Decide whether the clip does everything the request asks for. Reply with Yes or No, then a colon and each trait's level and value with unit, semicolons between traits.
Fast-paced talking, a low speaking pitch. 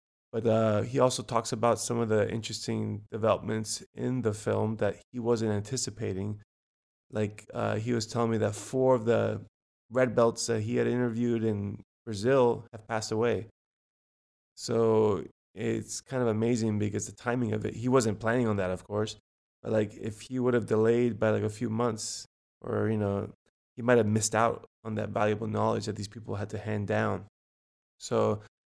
No: average, 185 wpm; low, 110 Hz